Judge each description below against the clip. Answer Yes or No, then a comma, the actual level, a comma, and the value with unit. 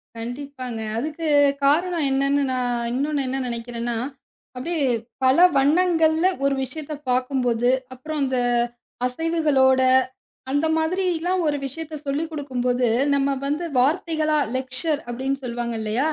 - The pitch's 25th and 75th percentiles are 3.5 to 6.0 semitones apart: Yes, average, 3.8 semitones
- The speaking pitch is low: No, very high, 275 Hz